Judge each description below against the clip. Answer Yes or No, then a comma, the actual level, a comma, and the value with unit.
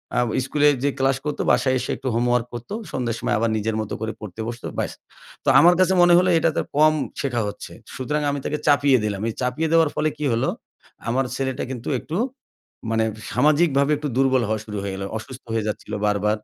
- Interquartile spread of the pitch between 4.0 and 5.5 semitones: Yes, average, 4.7 semitones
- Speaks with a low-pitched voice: Yes, low, 130 Hz